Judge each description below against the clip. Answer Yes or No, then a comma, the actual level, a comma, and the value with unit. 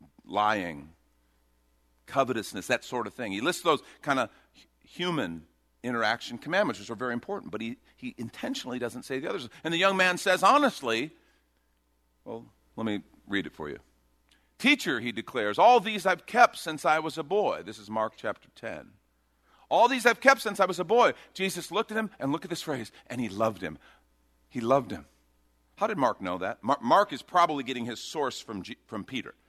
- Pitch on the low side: Yes, low, 125 Hz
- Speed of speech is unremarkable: Yes, average, 195 wpm